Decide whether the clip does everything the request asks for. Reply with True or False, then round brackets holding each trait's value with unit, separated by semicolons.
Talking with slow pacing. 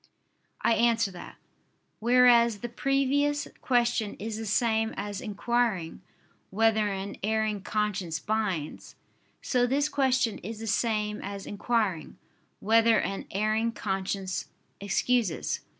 True (115 wpm)